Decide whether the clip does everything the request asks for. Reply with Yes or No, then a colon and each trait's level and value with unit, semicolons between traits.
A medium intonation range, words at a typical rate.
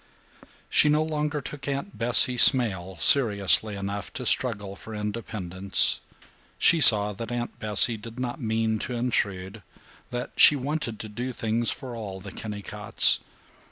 Yes: average, 3.6 semitones; average, 145 wpm